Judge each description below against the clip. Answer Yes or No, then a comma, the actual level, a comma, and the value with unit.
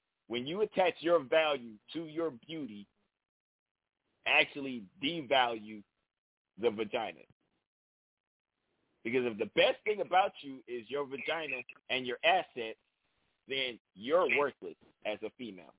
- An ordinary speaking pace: No, slow, 120 wpm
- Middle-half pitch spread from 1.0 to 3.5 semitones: No, wide, 5.6 semitones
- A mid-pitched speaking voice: No, low, 130 Hz